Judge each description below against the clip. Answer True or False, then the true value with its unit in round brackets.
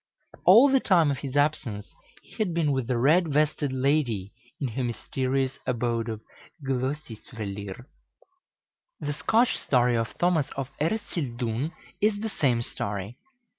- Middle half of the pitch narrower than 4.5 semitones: False (4.8 semitones)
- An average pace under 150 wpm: True (135 wpm)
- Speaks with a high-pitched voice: False (135 Hz)